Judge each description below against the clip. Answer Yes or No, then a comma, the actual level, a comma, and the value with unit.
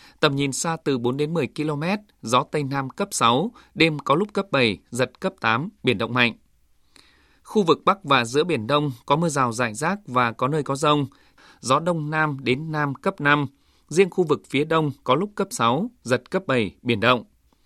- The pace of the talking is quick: No, average, 210 wpm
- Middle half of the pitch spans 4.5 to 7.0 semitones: Yes, average, 4.9 semitones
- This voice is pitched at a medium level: Yes, medium, 145 Hz